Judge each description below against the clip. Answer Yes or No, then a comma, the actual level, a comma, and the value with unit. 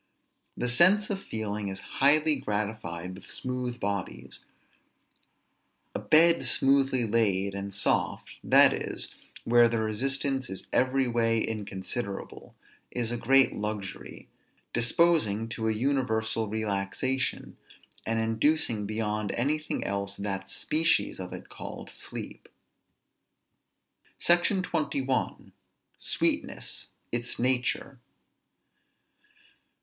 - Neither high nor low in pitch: No, low, 115 Hz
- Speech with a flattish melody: No, average, 4.6 semitones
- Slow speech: Yes, slow, 100 wpm